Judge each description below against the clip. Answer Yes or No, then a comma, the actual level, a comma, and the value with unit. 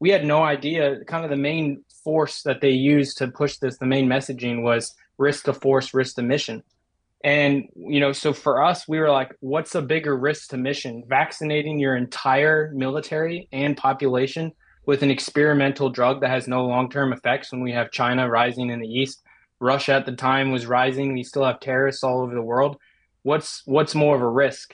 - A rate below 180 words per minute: No, average, 200 wpm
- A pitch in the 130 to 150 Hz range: Yes, low, 135 Hz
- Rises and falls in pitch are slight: Yes, narrow, 2.2 semitones